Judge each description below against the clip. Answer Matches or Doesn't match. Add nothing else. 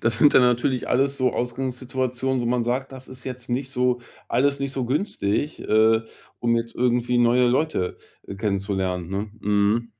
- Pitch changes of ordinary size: Doesn't match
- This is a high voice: Doesn't match